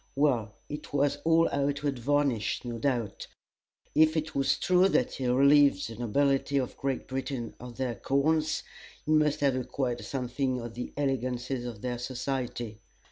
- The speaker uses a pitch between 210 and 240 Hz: No, low, 135 Hz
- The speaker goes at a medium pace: Yes, average, 160 wpm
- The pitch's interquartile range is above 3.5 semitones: No, average, 2.8 semitones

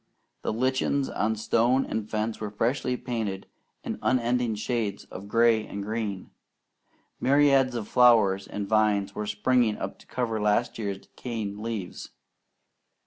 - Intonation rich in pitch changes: No, average, 2.9 semitones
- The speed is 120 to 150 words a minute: Yes, average, 140 wpm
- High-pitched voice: No, low, 110 Hz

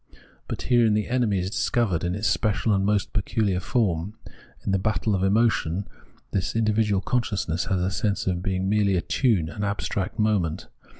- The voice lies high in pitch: No, low, 100 Hz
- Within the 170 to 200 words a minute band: Yes, average, 175 wpm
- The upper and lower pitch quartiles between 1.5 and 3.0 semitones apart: Yes, average, 2.7 semitones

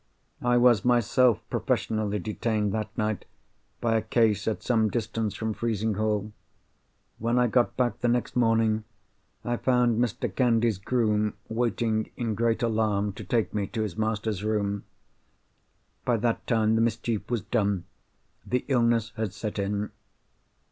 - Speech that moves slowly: No, average, 145 wpm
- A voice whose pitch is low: Yes, low, 110 Hz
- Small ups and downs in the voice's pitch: Yes, narrow, 2.0 semitones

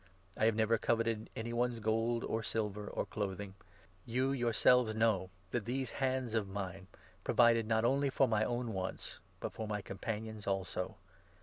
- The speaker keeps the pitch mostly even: Yes, narrow, 2.3 semitones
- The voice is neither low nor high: No, low, 110 Hz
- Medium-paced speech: Yes, average, 175 wpm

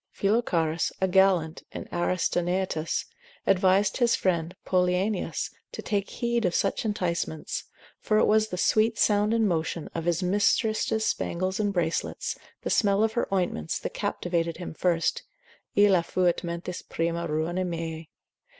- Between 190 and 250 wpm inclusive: No, average, 140 wpm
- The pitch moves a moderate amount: Yes, average, 3.3 semitones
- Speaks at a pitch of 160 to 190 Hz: Yes, medium, 185 Hz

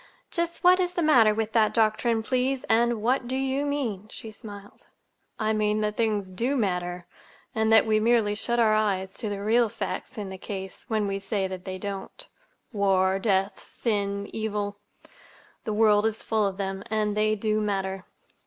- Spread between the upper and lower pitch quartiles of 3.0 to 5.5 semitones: No, narrow, 2.4 semitones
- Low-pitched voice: No, high, 215 Hz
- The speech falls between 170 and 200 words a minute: Yes, average, 180 wpm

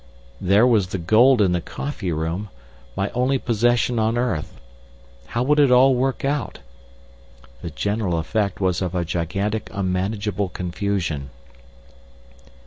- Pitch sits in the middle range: No, low, 100 Hz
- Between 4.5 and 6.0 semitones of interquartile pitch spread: Yes, average, 5.1 semitones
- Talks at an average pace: No, slow, 130 wpm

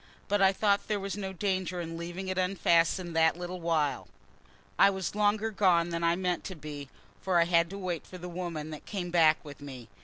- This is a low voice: No, medium, 175 Hz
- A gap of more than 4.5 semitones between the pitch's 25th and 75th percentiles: No, narrow, 2.4 semitones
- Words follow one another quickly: Yes, fast, 210 wpm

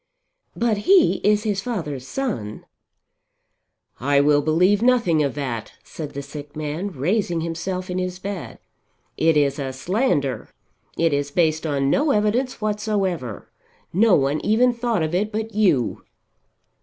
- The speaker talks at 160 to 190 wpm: No, average, 145 wpm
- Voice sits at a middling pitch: Yes, medium, 175 Hz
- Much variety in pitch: Yes, wide, 6.6 semitones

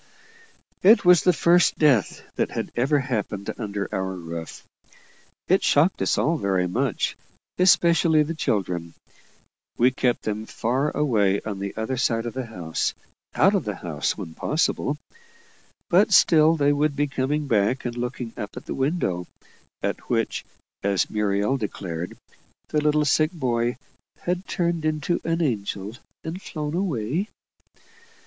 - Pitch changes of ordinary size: No, wide, 7.0 semitones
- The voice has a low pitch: Yes, low, 130 Hz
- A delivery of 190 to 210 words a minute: No, average, 145 wpm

